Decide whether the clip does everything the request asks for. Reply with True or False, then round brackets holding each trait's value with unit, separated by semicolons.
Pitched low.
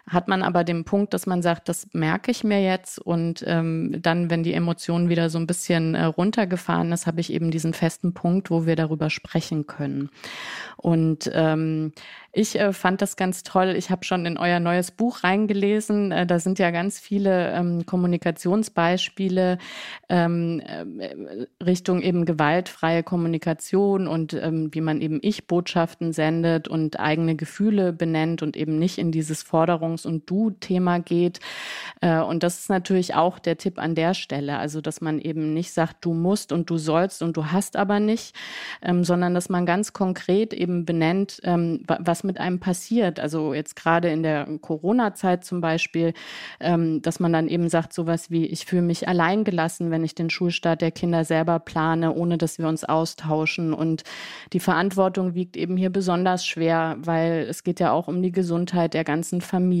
False (170 Hz)